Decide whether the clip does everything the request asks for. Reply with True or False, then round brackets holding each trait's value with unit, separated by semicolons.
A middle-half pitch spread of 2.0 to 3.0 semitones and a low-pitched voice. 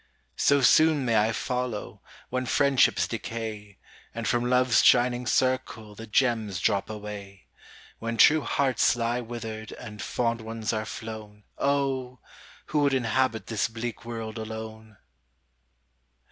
True (2.5 semitones; 115 Hz)